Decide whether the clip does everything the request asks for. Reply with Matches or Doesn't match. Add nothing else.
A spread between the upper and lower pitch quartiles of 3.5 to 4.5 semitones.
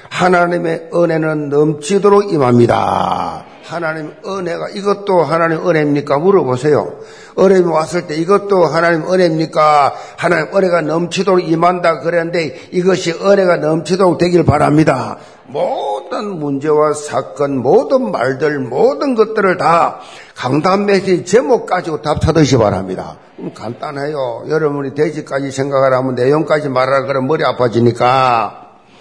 Matches